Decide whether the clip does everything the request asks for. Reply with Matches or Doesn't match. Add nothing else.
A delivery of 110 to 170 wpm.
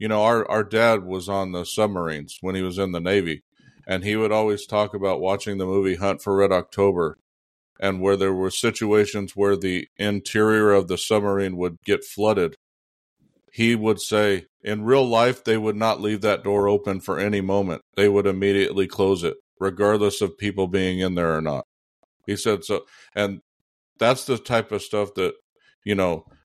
Doesn't match